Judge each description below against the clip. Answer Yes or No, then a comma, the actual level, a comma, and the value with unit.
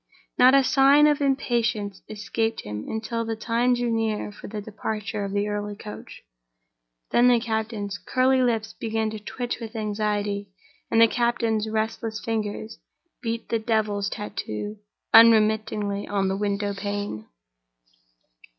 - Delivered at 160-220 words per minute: No, average, 140 wpm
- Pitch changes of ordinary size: No, narrow, 2.0 semitones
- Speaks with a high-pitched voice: Yes, high, 220 Hz